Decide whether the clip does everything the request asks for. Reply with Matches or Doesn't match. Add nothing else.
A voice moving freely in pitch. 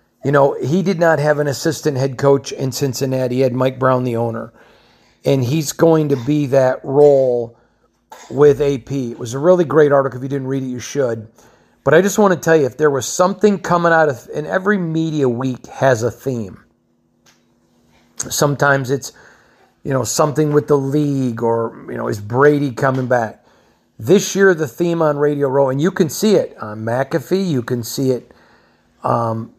Doesn't match